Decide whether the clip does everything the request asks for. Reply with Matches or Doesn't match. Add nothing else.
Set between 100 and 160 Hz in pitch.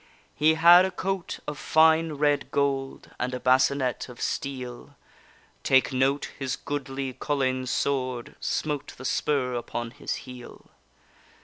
Matches